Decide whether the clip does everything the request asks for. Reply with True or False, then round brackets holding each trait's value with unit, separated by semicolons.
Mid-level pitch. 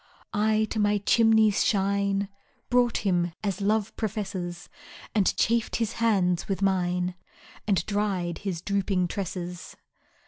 False (200 Hz)